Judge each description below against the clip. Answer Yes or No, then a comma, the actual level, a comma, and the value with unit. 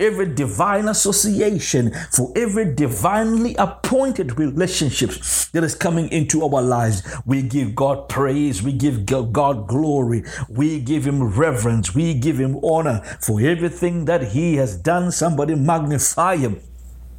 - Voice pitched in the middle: Yes, medium, 145 Hz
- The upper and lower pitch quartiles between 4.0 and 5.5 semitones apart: Yes, average, 4.8 semitones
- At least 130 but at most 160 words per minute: Yes, slow, 135 wpm